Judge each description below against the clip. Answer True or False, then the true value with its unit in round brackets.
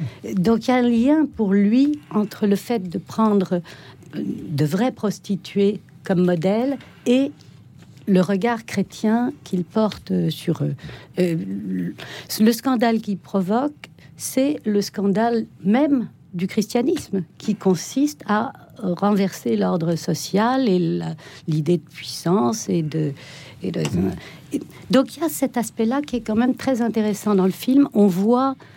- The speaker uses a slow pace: True (140 wpm)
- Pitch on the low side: False (200 Hz)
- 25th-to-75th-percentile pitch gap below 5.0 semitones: False (5.3 semitones)